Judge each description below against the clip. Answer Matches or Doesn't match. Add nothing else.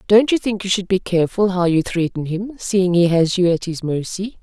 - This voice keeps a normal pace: Doesn't match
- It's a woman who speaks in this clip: Matches